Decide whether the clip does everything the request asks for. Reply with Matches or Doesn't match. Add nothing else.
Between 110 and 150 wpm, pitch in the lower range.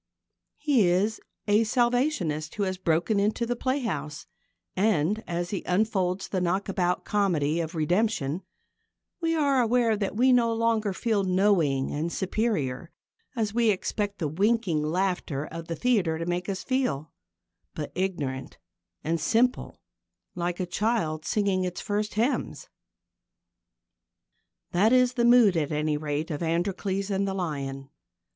Doesn't match